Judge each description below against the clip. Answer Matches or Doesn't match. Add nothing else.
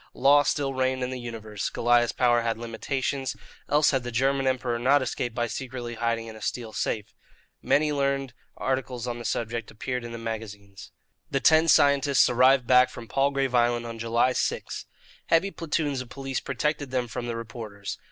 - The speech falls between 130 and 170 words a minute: Doesn't match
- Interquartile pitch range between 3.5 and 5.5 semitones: Doesn't match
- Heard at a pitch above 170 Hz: Doesn't match